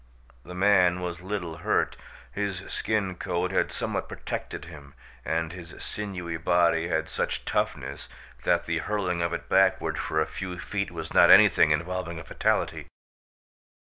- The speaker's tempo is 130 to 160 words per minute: Yes, average, 150 wpm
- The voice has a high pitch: No, very low, 90 Hz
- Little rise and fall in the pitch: Yes, narrow, 2.3 semitones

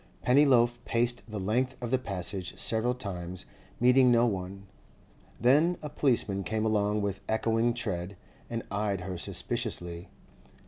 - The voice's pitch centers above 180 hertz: No, low, 110 Hz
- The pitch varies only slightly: No, average, 3.9 semitones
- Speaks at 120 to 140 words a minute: Yes, slow, 135 wpm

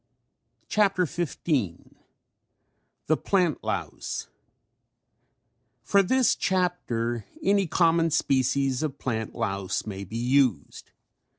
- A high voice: No, medium, 140 Hz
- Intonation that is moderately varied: No, wide, 7.5 semitones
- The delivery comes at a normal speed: No, slow, 95 wpm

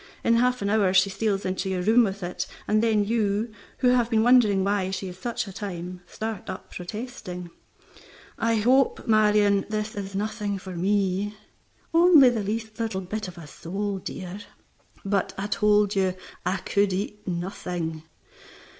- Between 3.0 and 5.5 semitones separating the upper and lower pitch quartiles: No, narrow, 2.6 semitones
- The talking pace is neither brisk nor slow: Yes, average, 165 wpm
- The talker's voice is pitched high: Yes, high, 205 Hz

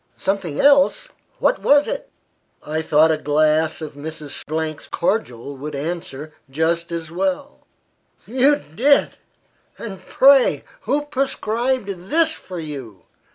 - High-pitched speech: No, medium, 170 Hz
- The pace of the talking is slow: Yes, slow, 120 wpm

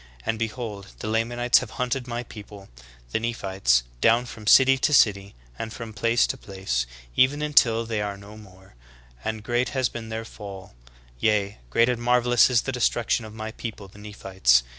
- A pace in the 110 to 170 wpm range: No, average, 185 wpm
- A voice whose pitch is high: No, low, 110 Hz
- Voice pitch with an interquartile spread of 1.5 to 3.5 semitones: Yes, average, 3.1 semitones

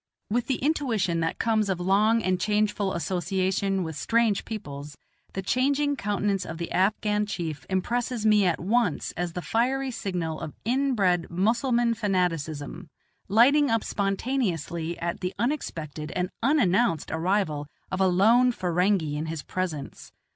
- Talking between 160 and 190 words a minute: No, average, 140 wpm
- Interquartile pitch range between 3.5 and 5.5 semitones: Yes, average, 5.1 semitones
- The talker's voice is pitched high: Yes, high, 195 Hz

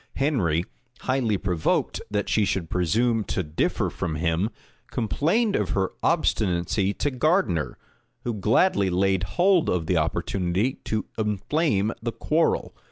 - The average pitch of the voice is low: Yes, low, 100 Hz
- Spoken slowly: Yes, slow, 130 wpm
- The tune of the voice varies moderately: No, wide, 5.9 semitones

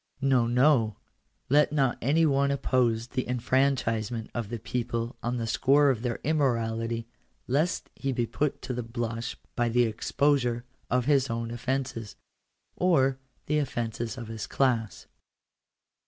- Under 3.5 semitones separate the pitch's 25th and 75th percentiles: Yes, average, 2.9 semitones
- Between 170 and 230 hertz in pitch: No, low, 120 Hz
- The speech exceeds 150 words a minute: No, average, 140 wpm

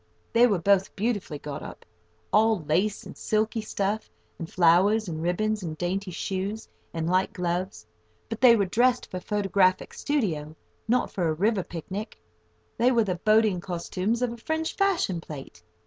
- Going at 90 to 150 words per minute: No, average, 165 wpm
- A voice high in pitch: Yes, high, 195 Hz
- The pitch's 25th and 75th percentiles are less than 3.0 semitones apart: No, average, 4.2 semitones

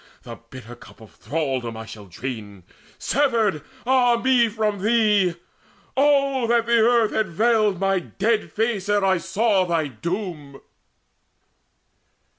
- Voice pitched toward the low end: No, high, 205 Hz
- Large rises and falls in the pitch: Yes, wide, 7.4 semitones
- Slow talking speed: Yes, slow, 130 wpm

